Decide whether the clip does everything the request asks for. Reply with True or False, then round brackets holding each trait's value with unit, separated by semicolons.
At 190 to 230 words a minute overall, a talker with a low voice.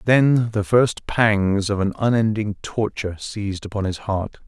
False (160 wpm; 105 Hz)